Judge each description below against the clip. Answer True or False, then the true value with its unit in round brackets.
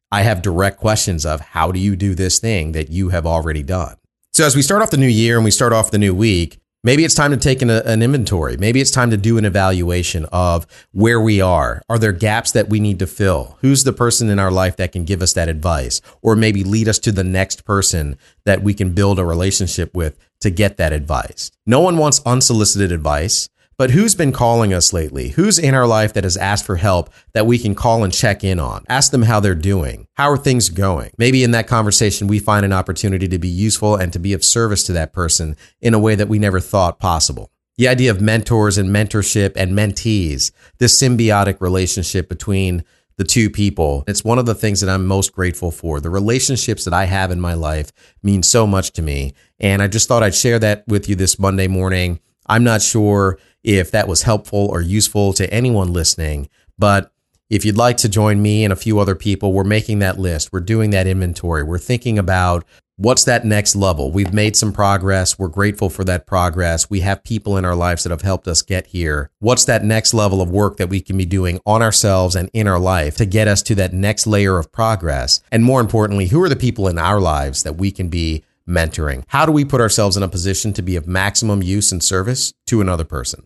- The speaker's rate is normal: False (230 wpm)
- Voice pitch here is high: False (100 Hz)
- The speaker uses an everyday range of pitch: True (3.3 semitones)